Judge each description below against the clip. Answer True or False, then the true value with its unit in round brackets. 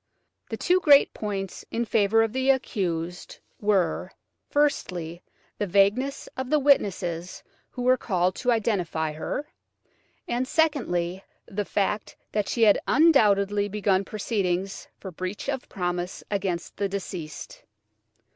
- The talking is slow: True (125 wpm)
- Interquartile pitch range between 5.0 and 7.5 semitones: True (5.3 semitones)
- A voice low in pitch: False (200 Hz)